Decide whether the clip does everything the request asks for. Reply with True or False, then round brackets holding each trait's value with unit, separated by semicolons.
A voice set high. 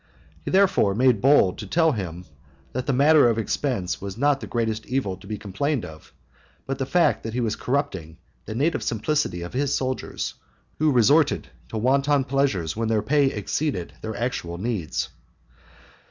False (120 Hz)